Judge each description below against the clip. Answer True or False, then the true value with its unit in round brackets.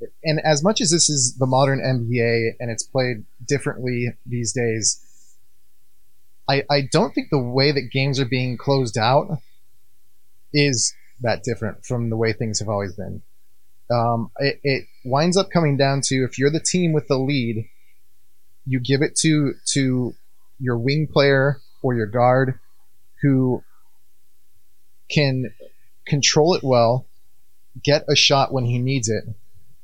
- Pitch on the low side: True (125 Hz)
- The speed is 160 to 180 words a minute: False (150 wpm)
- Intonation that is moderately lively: True (3.5 semitones)